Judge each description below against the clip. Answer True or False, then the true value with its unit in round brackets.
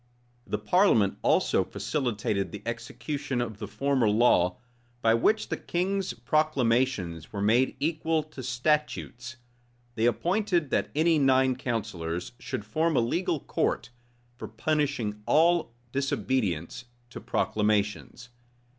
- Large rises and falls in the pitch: True (6.0 semitones)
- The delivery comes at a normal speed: False (120 wpm)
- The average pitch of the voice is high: False (125 Hz)